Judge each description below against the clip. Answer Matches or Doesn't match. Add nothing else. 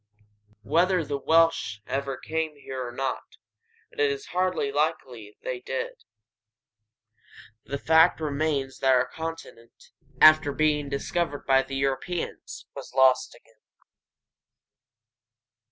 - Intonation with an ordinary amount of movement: Matches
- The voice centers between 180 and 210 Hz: Doesn't match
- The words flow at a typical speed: Doesn't match